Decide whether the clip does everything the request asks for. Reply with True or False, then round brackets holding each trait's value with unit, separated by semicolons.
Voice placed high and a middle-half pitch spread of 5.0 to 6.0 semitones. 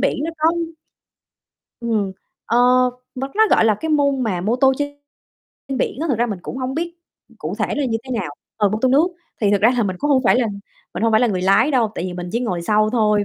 False (235 Hz; 4.5 semitones)